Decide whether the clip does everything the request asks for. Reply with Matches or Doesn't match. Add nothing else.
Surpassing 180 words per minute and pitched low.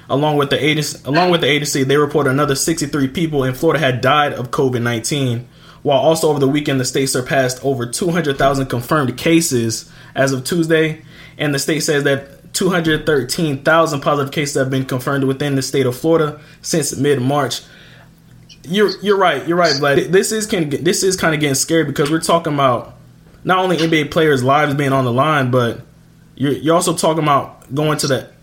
Doesn't match